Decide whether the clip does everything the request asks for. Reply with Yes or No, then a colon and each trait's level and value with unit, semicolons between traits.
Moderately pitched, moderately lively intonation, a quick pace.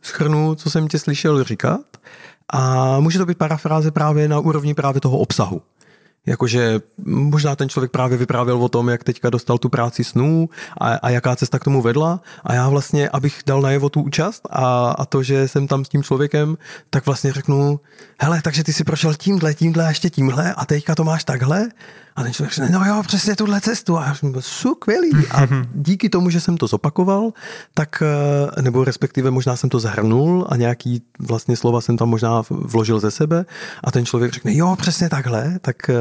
Yes: medium, 145 Hz; average, 4.1 semitones; fast, 200 wpm